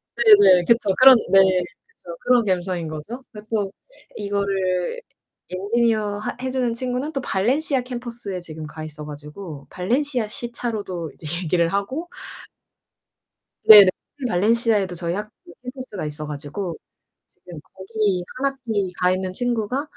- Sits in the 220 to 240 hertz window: No, high, 205 Hz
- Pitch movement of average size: Yes, average, 4.9 semitones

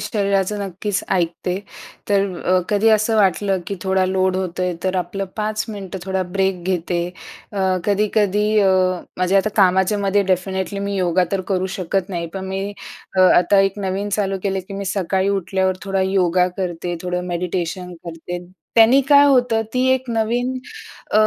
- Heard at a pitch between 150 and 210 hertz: Yes, high, 190 Hz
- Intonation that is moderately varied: No, narrow, 1.9 semitones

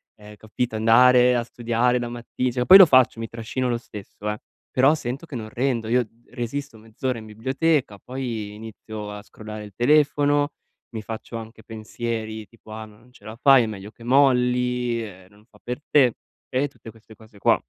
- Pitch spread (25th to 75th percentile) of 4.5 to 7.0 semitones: No, narrow, 2.5 semitones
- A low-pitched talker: Yes, low, 115 Hz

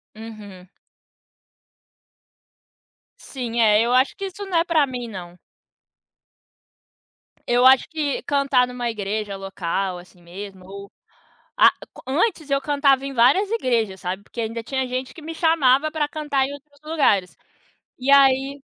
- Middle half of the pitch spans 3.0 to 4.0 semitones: No, wide, 5.5 semitones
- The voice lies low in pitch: No, very high, 255 Hz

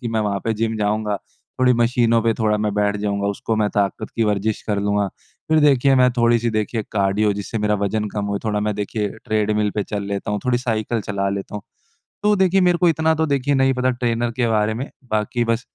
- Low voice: Yes, low, 110 Hz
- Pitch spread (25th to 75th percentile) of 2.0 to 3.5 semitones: Yes, average, 2.9 semitones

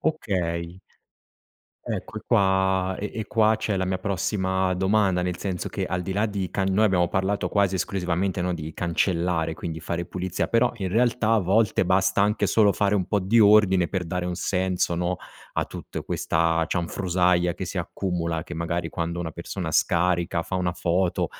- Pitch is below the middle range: Yes, very low, 95 Hz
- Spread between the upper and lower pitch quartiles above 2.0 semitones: Yes, narrow, 2.4 semitones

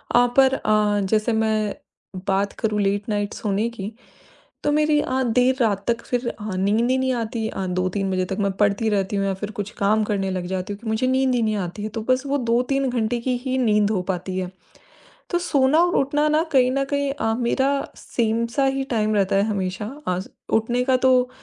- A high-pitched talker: Yes, high, 220 Hz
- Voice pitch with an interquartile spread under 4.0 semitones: No, average, 4.3 semitones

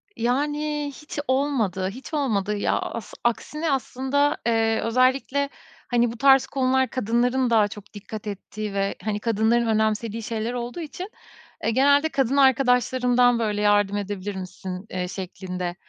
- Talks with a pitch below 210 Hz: No, high, 235 Hz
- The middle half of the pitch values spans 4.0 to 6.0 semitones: Yes, average, 4.3 semitones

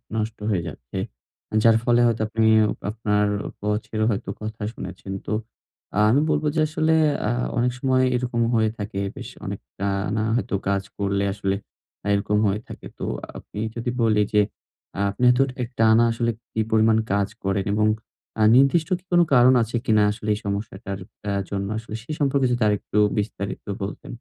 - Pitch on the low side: Yes, low, 110 Hz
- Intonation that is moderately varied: Yes, average, 3.0 semitones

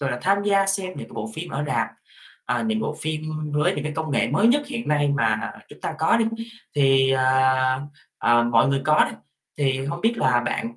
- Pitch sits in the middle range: Yes, medium, 145 Hz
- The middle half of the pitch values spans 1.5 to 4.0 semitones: No, average, 5.2 semitones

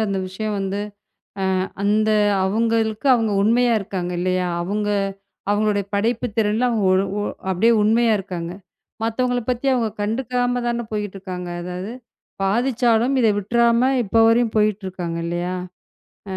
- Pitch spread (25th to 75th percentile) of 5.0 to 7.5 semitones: No, average, 3.5 semitones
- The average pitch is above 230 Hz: No, high, 215 Hz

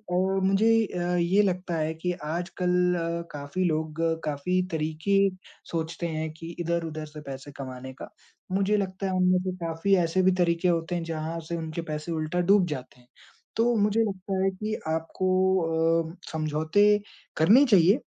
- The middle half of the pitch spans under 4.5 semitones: Yes, average, 2.9 semitones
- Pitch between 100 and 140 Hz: No, medium, 170 Hz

